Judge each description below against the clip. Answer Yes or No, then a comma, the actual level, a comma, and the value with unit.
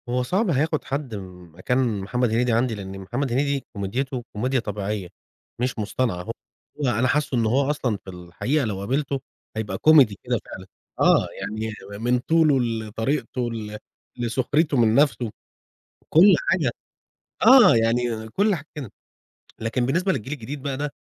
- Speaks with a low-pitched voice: Yes, low, 125 Hz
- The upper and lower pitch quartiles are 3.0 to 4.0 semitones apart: No, average, 4.4 semitones